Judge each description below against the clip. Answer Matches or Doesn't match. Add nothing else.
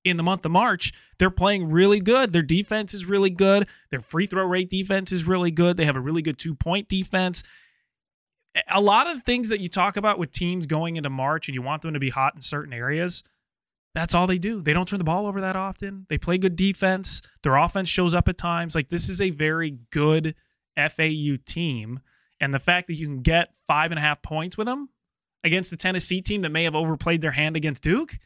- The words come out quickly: Matches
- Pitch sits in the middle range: Matches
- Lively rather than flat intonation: Doesn't match